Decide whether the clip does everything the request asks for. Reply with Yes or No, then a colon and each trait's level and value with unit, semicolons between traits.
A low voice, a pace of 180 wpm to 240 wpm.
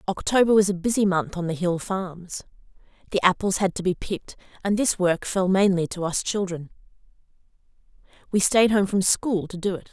No: high, 190 Hz; average, 190 wpm